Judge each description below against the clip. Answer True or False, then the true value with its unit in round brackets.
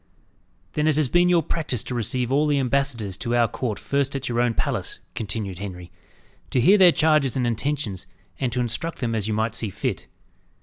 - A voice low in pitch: True (125 Hz)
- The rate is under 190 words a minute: False (205 wpm)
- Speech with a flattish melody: False (4.5 semitones)